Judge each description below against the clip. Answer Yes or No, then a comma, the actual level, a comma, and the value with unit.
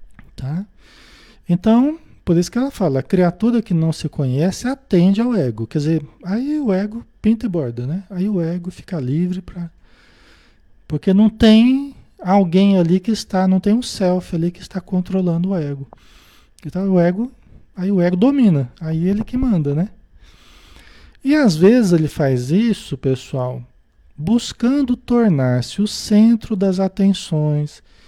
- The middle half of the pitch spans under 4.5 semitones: No, average, 5.2 semitones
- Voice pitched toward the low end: No, medium, 185 Hz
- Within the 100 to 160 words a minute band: Yes, average, 155 wpm